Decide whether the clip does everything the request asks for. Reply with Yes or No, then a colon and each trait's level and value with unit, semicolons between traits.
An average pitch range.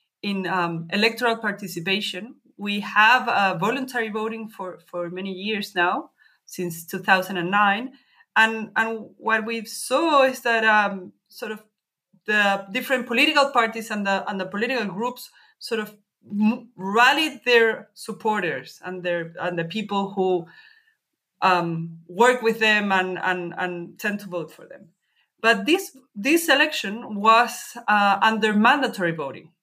Yes: average, 3.9 semitones